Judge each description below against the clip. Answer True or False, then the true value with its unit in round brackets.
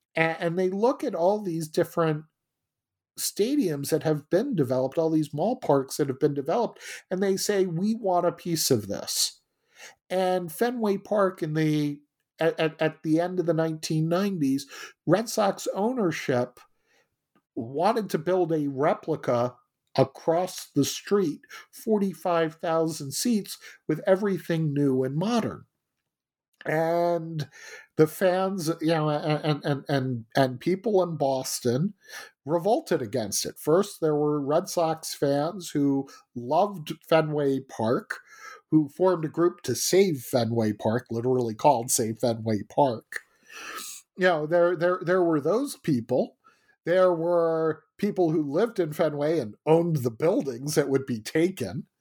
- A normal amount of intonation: True (4.2 semitones)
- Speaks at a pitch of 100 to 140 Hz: False (165 Hz)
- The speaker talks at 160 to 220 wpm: False (140 wpm)